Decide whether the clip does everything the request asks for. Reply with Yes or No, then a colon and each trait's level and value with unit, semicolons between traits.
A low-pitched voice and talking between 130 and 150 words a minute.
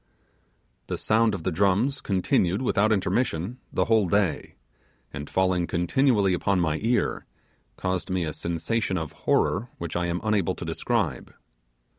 Yes: very low, 95 Hz; average, 145 wpm